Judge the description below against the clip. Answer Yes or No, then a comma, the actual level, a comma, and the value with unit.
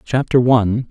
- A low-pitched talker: Yes, low, 120 Hz